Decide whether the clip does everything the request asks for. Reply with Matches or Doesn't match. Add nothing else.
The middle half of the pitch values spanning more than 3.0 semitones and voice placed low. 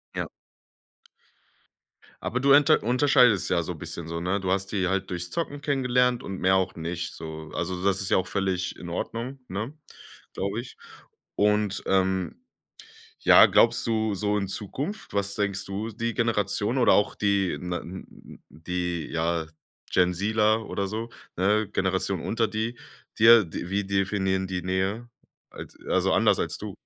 Matches